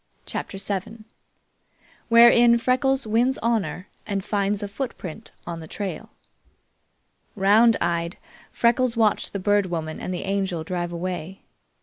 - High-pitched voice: Yes, high, 200 Hz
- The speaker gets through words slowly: Yes, slow, 125 wpm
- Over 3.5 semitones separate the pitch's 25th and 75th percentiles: Yes, average, 4.4 semitones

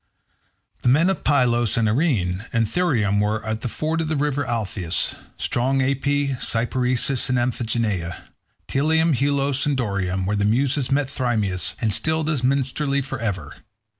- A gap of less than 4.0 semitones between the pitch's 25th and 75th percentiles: No, average, 4.5 semitones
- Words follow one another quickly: No, average, 155 wpm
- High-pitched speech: No, low, 125 Hz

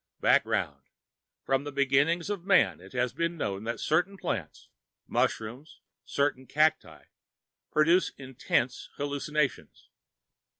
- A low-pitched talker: No, medium, 145 Hz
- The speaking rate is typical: No, slow, 110 wpm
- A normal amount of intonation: Yes, average, 4.3 semitones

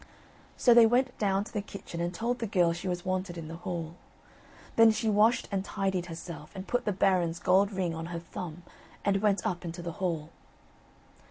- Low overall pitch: No, medium, 185 Hz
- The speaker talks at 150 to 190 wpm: No, average, 200 wpm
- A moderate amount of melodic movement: Yes, average, 3.0 semitones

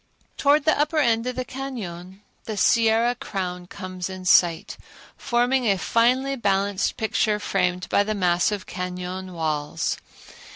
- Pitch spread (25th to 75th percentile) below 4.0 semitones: No, average, 4.8 semitones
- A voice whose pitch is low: No, high, 200 Hz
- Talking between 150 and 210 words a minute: No, slow, 135 wpm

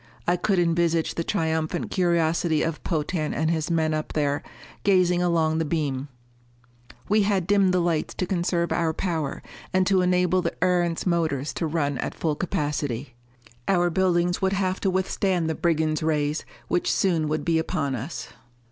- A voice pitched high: No, medium, 170 Hz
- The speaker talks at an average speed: Yes, average, 165 wpm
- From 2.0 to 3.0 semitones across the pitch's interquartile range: Yes, narrow, 2.6 semitones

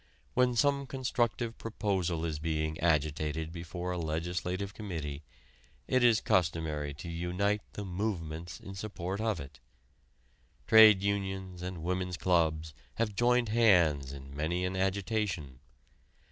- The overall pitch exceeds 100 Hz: No, very low, 90 Hz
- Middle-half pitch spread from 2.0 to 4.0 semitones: No, average, 4.5 semitones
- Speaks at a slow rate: Yes, slow, 125 wpm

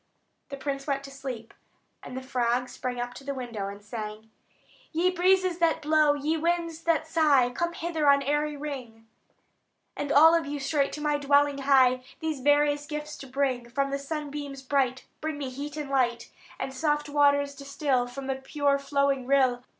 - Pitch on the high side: Yes, very high, 280 Hz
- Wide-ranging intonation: No, narrow, 2.4 semitones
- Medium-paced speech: Yes, average, 180 wpm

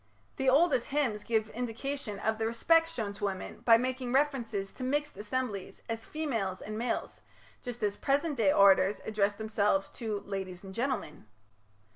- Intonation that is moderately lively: Yes, average, 4.4 semitones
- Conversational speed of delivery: Yes, average, 160 wpm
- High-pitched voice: Yes, high, 225 Hz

